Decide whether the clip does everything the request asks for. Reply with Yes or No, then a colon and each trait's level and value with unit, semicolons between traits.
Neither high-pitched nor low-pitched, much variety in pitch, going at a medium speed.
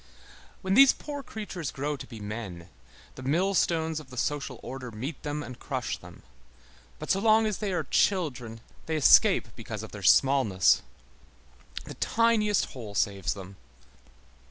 Yes: medium, 145 Hz; wide, 8.8 semitones; average, 155 wpm